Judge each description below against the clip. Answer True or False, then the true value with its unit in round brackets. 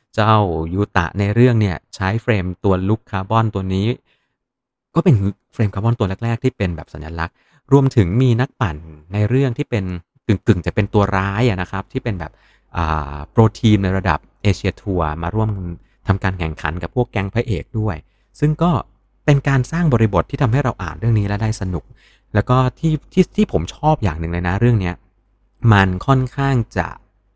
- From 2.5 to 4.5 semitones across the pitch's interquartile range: False (5.1 semitones)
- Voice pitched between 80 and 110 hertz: True (105 Hz)